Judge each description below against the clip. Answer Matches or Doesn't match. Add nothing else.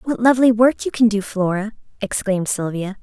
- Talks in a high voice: Matches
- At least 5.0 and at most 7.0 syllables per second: Matches